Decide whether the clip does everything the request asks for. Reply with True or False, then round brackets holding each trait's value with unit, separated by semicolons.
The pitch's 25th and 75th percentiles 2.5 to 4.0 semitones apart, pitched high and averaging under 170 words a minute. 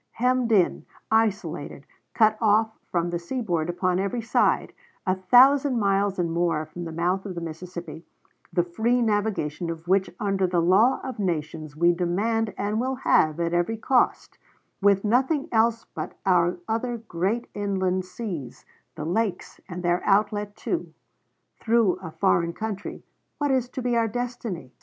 False (4.6 semitones; 195 Hz; 155 wpm)